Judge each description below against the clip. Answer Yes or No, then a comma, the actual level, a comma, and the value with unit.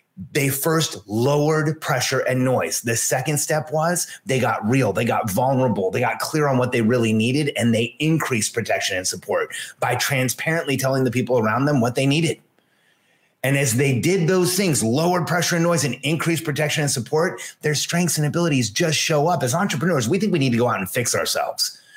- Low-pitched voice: No, medium, 145 Hz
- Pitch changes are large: No, average, 4.6 semitones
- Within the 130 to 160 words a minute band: No, average, 200 wpm